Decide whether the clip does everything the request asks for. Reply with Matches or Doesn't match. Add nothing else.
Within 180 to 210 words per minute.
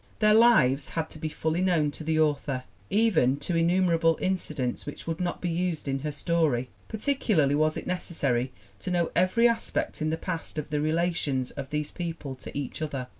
Matches